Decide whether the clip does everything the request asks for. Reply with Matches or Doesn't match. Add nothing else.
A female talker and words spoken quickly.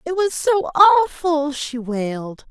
Doesn't match